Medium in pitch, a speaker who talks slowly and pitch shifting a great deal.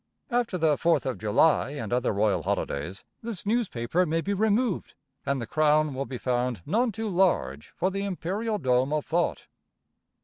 No: medium, 155 Hz; average, 170 wpm; wide, 8.0 semitones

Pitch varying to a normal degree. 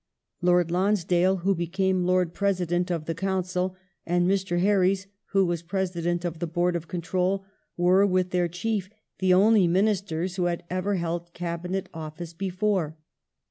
No: narrow, 1.7 semitones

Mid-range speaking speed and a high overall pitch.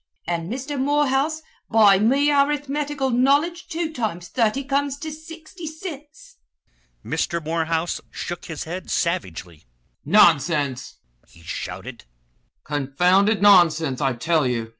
No: slow, 115 wpm; high, 210 Hz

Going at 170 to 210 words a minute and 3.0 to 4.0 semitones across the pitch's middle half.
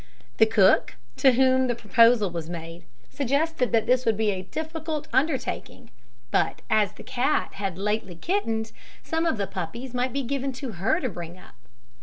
No: average, 175 wpm; average, 5.2 semitones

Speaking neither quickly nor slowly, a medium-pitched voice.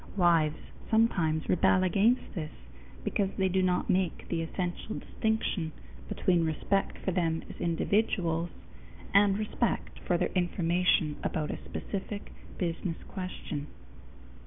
No: slow, 120 wpm; medium, 180 Hz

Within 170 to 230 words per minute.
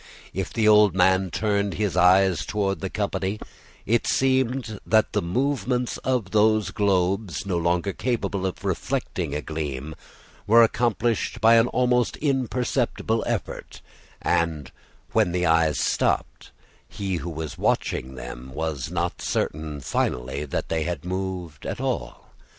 No: average, 140 wpm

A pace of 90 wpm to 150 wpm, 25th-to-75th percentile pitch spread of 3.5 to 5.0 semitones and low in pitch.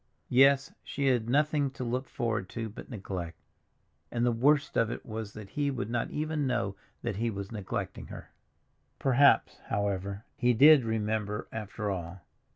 No: average, 160 wpm; average, 4.6 semitones; low, 115 Hz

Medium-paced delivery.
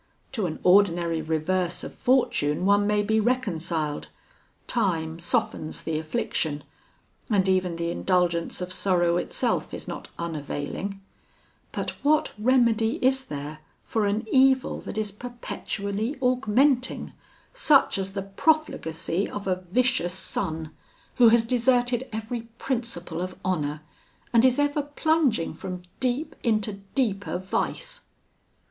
No: slow, 125 wpm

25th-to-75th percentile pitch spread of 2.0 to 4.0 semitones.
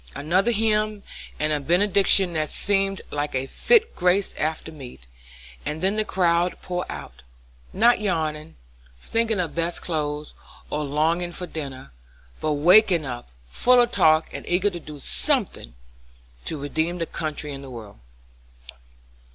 No: average, 4.7 semitones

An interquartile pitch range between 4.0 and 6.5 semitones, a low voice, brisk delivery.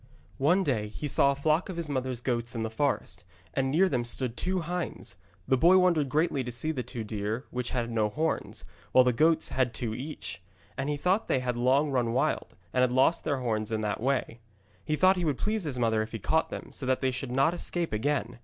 Yes: average, 4.7 semitones; low, 130 Hz; fast, 235 wpm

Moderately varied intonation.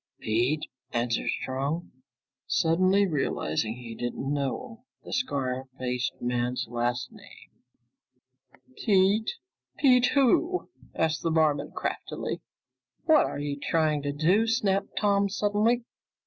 No: wide, 8.4 semitones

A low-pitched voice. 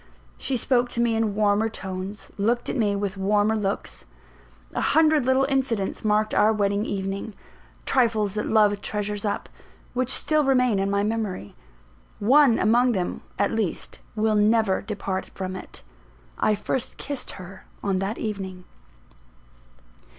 No: high, 210 Hz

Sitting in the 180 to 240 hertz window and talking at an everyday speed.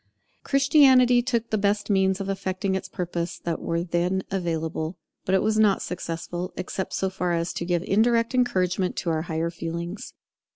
Yes: medium, 185 Hz; average, 170 wpm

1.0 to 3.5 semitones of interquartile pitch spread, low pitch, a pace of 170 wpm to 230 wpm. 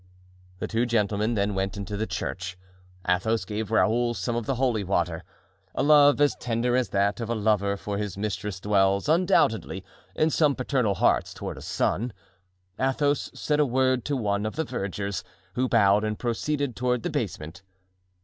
No: average, 4.1 semitones; low, 110 Hz; average, 175 wpm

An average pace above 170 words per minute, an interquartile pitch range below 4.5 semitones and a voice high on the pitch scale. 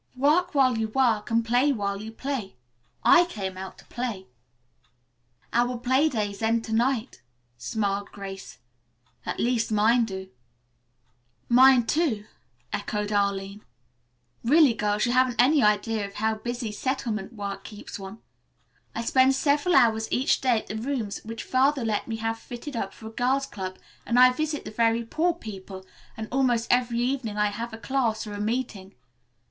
No: average, 165 wpm; average, 3.5 semitones; high, 230 Hz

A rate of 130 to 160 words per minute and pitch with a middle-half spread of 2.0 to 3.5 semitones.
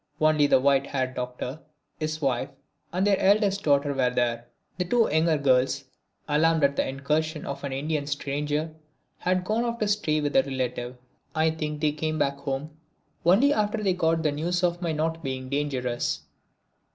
No: average, 175 wpm; average, 3.2 semitones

